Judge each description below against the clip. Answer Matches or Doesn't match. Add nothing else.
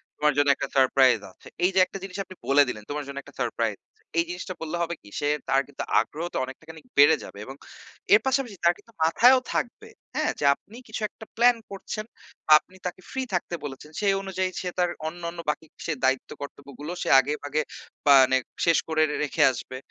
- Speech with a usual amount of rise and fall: Matches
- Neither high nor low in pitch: Matches